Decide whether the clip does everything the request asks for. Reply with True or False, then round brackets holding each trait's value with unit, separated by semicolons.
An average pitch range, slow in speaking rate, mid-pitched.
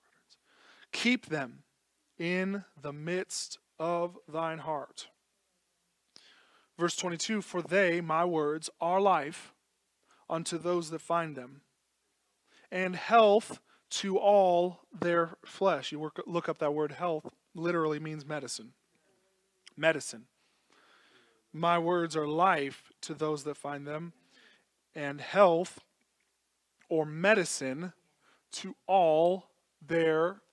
True (3.0 semitones; 105 wpm; 170 Hz)